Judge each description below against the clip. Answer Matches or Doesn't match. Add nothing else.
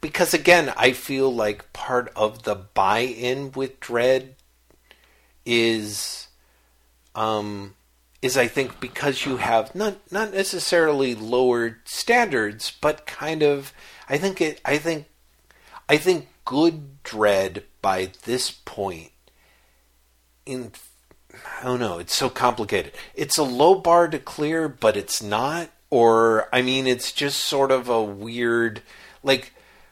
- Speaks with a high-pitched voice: Doesn't match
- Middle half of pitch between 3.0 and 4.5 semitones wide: Doesn't match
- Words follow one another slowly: Matches